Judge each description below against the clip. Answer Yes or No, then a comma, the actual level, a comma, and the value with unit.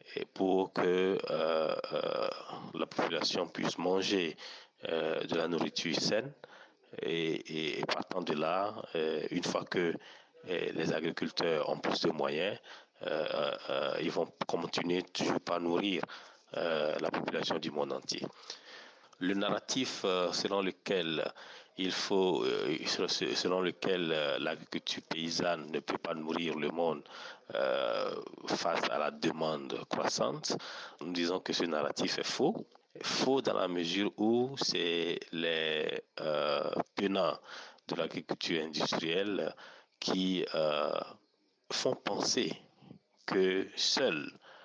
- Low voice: Yes, very low, 95 Hz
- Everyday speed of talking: No, slow, 120 wpm